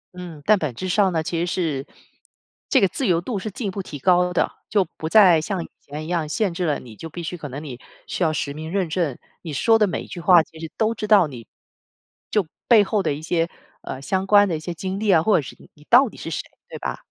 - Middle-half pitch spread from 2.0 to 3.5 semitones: No, average, 4.1 semitones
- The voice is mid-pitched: Yes, medium, 175 Hz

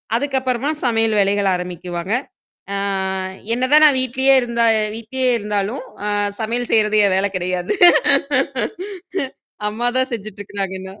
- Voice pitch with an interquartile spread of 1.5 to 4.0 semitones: No, average, 4.5 semitones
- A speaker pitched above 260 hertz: No, high, 220 Hz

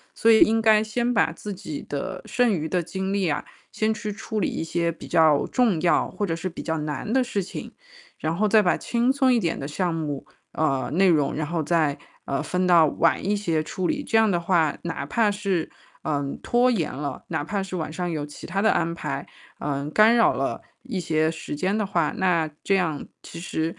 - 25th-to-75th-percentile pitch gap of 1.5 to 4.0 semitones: No, average, 4.9 semitones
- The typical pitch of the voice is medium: Yes, medium, 175 Hz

